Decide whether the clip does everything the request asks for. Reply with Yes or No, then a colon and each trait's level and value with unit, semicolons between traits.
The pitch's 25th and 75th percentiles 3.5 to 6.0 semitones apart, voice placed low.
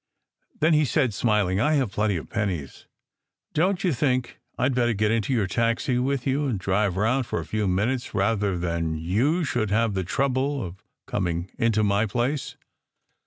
Yes: average, 5.0 semitones; low, 115 Hz